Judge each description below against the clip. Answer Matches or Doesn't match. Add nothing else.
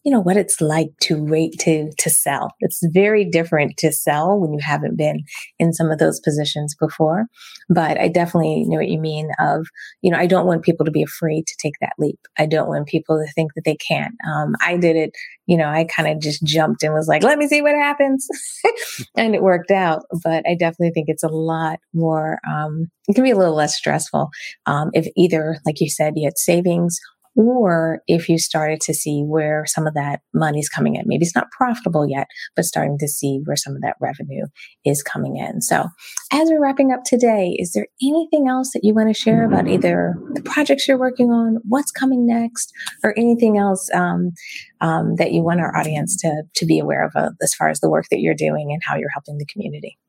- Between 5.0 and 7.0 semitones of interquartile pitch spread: Matches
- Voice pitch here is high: Doesn't match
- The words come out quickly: Matches